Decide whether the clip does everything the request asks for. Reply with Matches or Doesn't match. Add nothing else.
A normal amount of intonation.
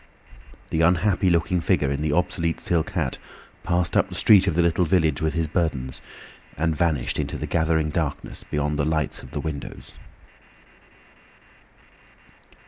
Doesn't match